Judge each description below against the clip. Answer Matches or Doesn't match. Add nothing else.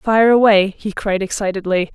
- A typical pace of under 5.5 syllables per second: Matches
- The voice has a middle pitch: Doesn't match